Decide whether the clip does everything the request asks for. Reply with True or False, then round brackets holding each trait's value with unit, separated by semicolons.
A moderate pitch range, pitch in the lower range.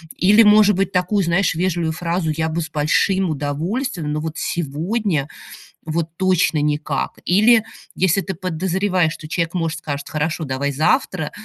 False (3.4 semitones; 170 Hz)